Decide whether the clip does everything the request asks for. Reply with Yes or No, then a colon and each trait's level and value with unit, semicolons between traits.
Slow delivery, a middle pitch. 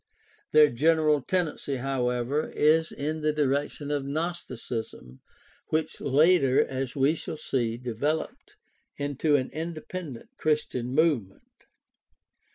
Yes: slow, 110 wpm; medium, 145 Hz